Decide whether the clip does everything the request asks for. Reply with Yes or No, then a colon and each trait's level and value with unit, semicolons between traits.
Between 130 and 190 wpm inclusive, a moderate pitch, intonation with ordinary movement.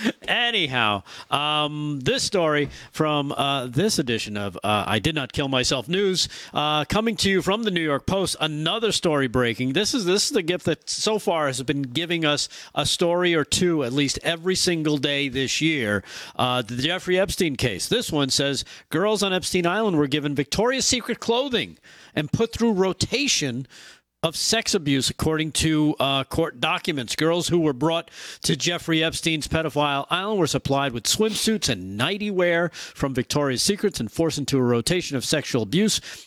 Yes: average, 180 wpm; medium, 155 Hz; average, 4.7 semitones